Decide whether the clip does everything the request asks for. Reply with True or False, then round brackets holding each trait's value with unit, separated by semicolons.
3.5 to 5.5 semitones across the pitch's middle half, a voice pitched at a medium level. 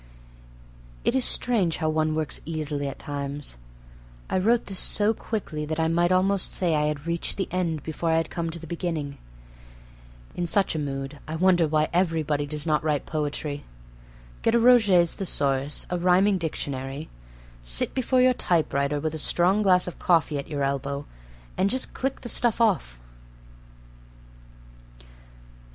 True (4.1 semitones; 160 Hz)